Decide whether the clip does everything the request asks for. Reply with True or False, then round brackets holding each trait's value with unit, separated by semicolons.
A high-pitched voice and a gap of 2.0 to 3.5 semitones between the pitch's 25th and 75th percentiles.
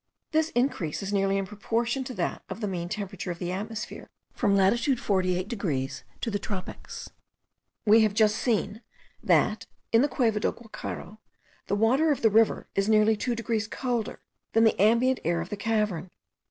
True (215 Hz; 3.0 semitones)